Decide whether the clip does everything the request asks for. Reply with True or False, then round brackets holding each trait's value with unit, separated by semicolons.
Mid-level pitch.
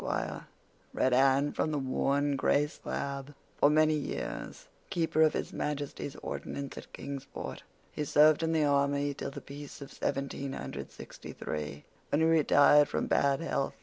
True (145 Hz)